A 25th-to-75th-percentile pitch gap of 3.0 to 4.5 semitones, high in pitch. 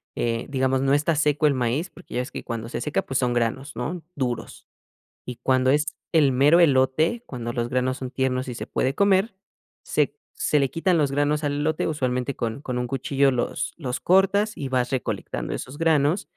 No: average, 3.4 semitones; low, 135 Hz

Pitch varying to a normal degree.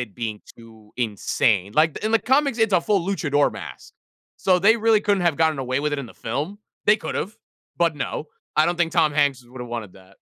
No: wide, 8.3 semitones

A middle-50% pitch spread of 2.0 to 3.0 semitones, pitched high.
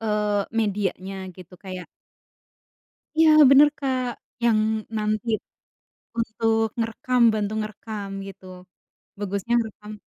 Yes: narrow, 2.4 semitones; high, 215 Hz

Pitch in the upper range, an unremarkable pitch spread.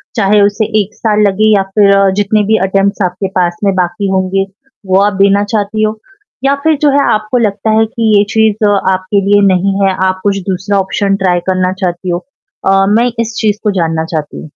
No: high, 200 Hz; narrow, 2.2 semitones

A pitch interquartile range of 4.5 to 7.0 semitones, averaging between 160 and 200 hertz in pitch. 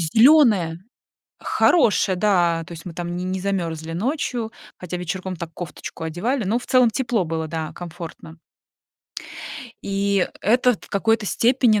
Yes: average, 4.9 semitones; high, 190 Hz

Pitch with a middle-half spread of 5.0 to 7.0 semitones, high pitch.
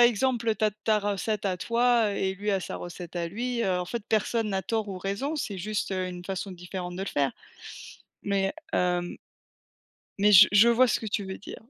No: average, 3.2 semitones; high, 200 Hz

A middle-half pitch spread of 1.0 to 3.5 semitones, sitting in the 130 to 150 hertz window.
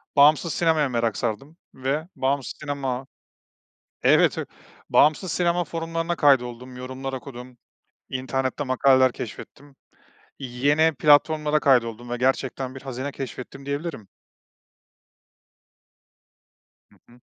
Yes: average, 2.8 semitones; low, 135 Hz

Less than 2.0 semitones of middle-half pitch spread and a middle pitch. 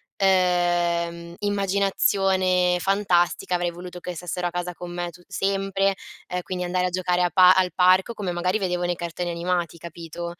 Yes: narrow, 1.1 semitones; medium, 180 Hz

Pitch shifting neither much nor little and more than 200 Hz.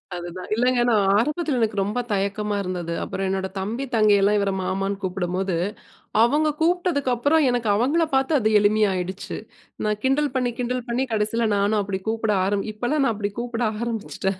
Yes: average, 4.2 semitones; high, 215 Hz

